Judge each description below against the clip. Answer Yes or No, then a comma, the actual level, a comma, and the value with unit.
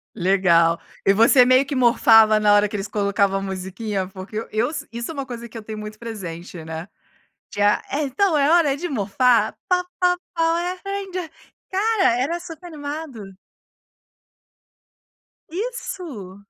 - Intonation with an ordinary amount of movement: No, wide, 8.1 semitones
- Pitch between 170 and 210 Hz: No, high, 235 Hz